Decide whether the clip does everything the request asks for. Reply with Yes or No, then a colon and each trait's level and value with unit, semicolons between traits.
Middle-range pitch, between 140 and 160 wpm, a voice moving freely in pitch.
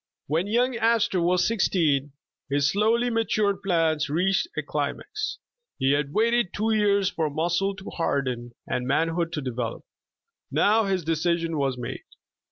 Yes: medium, 175 Hz; average, 150 wpm; wide, 6.3 semitones